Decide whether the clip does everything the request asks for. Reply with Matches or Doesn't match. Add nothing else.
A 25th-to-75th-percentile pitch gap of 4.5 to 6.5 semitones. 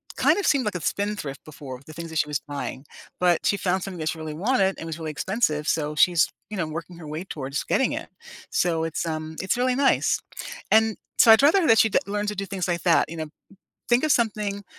Matches